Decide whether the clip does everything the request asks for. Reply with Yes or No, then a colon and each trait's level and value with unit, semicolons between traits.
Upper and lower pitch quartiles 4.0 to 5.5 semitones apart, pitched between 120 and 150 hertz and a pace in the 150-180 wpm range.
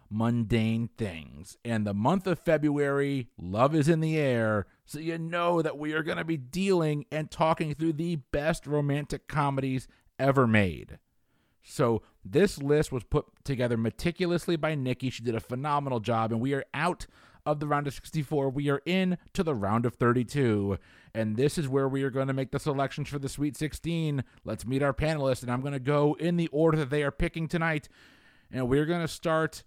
No: average, 4.6 semitones; medium, 140 Hz; average, 200 wpm